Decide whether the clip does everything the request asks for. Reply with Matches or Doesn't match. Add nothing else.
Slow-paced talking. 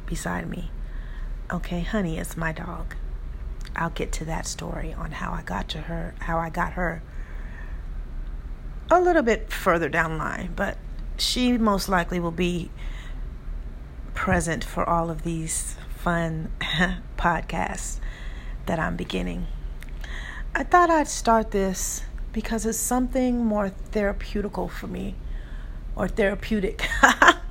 Matches